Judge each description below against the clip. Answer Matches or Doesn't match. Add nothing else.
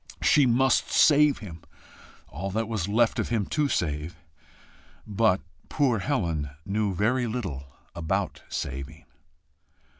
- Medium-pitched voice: Doesn't match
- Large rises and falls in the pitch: Matches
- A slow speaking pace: Matches